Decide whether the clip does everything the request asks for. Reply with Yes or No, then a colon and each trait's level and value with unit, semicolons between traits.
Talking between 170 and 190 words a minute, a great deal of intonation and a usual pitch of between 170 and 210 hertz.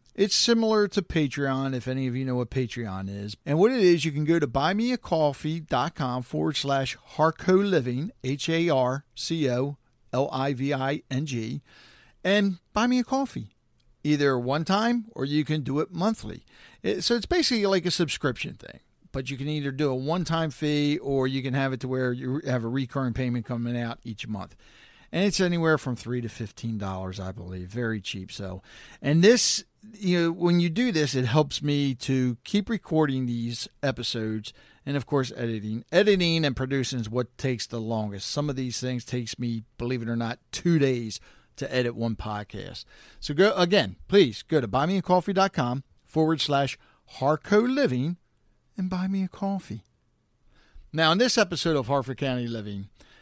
No: average, 185 wpm; wide, 5.8 semitones; medium, 140 Hz